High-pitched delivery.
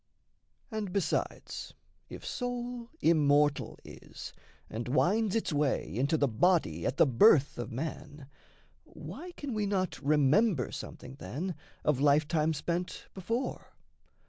No: medium, 155 Hz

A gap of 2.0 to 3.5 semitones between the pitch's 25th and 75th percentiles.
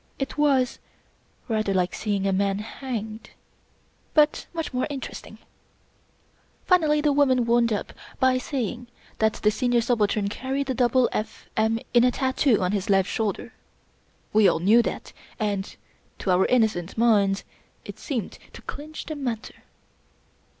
No: average, 4.1 semitones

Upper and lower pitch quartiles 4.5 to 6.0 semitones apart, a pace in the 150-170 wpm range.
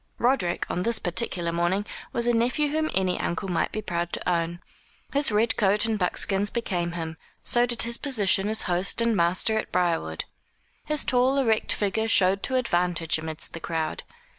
No: average, 5.2 semitones; average, 180 wpm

